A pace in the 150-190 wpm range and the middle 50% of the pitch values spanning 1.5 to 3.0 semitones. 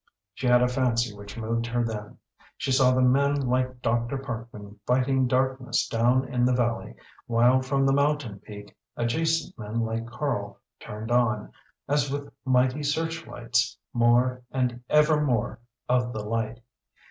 Yes: average, 155 wpm; narrow, 2.5 semitones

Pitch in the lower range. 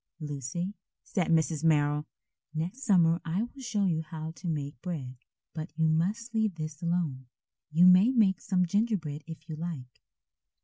No: medium, 165 Hz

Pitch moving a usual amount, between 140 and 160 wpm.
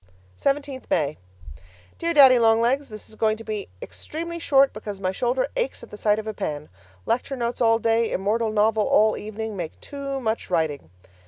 No: average, 4.1 semitones; average, 185 wpm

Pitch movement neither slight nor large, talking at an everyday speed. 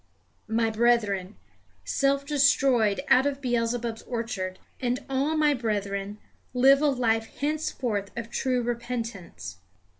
No: average, 3.8 semitones; slow, 115 wpm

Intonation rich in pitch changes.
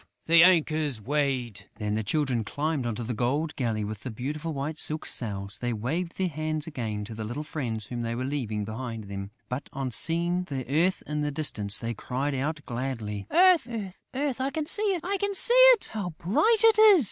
Yes: wide, 6.5 semitones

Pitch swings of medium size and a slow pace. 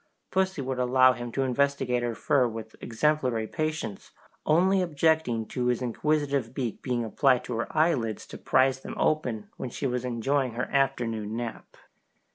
No: average, 3.3 semitones; average, 160 wpm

